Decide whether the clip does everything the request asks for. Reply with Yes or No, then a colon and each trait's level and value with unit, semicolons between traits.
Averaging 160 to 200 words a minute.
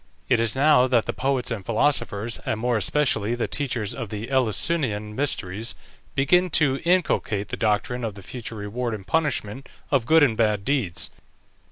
Yes: average, 170 wpm